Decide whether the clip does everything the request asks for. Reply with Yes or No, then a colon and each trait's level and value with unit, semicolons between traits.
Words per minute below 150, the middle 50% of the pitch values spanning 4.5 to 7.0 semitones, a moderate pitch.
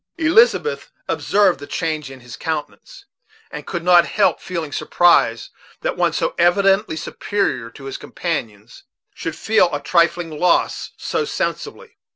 Yes: average, 140 wpm; average, 5.3 semitones; medium, 170 Hz